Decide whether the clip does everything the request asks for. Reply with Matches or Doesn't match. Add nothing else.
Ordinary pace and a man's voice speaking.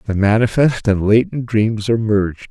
Matches